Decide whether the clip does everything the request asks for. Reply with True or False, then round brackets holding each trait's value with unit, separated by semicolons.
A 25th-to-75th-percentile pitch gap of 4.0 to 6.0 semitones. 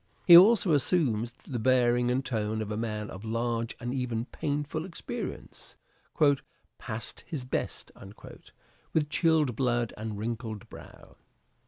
True (4.4 semitones)